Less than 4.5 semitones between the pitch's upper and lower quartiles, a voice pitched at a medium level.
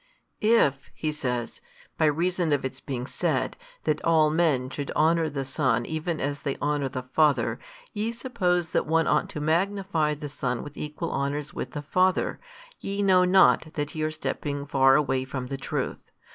Yes: average, 3.5 semitones; medium, 150 Hz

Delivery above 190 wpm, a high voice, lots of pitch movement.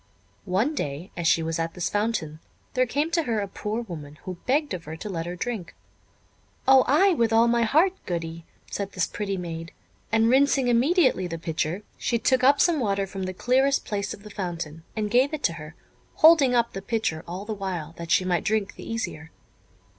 Yes: fast, 205 wpm; high, 205 Hz; wide, 6.5 semitones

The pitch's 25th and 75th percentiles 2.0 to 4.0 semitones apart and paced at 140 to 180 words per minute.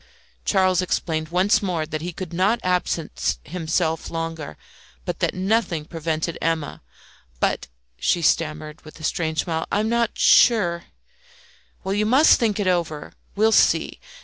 Yes: average, 3.6 semitones; average, 150 wpm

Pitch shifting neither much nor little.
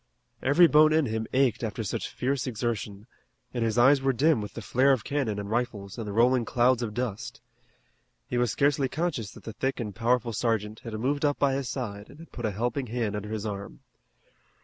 Yes: average, 3.7 semitones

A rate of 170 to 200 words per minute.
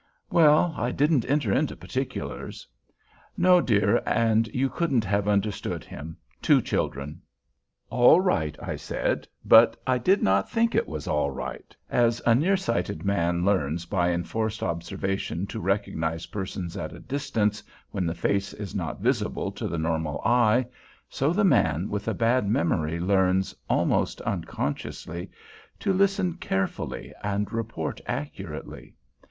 No: average, 140 wpm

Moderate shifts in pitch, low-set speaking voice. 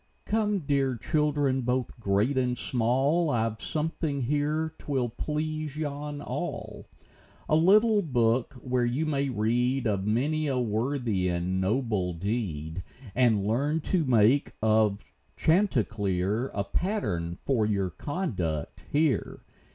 No: wide, 5.8 semitones; low, 125 Hz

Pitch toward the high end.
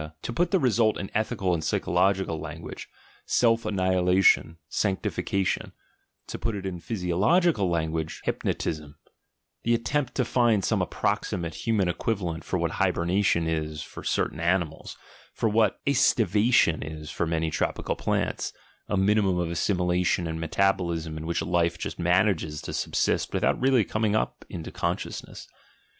No: very low, 90 Hz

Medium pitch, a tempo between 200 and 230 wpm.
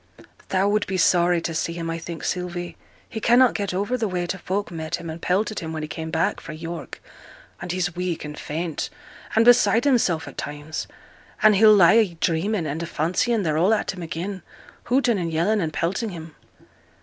Yes: medium, 175 Hz; fast, 205 wpm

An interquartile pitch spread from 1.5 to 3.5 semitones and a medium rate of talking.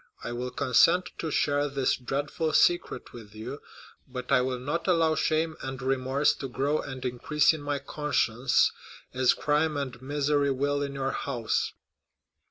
Yes: narrow, 2.6 semitones; average, 160 wpm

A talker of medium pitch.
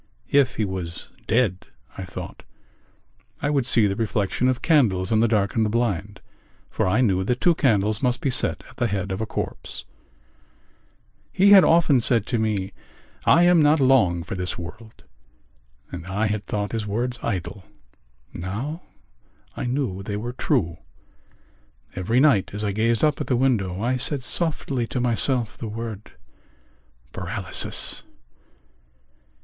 No: low, 110 Hz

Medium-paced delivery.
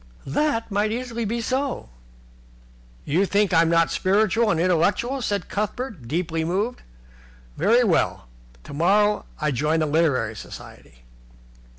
No: slow, 120 wpm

